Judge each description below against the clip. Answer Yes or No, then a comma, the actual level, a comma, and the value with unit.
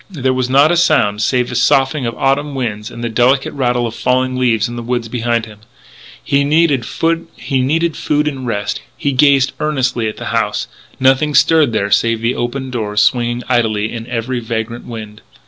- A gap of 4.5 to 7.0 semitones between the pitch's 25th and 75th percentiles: No, average, 3.0 semitones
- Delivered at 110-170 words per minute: No, average, 180 wpm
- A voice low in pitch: Yes, low, 125 Hz